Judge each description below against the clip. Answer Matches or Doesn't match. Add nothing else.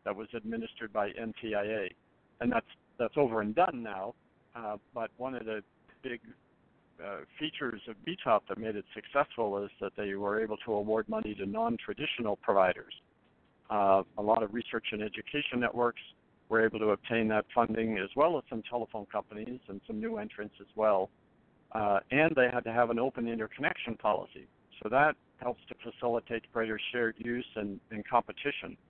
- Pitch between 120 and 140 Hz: Doesn't match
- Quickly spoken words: Doesn't match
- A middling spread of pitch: Doesn't match